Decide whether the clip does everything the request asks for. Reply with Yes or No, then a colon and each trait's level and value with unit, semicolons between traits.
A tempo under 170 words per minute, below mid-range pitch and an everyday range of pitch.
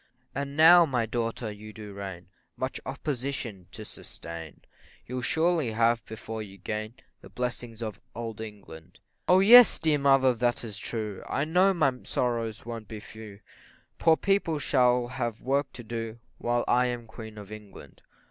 Yes: average, 160 wpm; low, 120 Hz; average, 4.0 semitones